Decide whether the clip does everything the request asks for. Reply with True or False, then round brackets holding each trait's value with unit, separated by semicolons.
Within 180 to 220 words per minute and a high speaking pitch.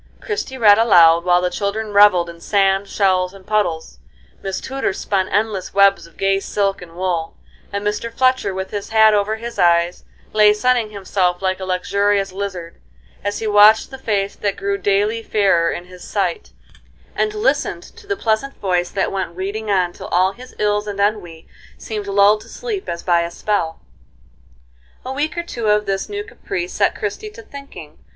True (185 wpm; 200 Hz)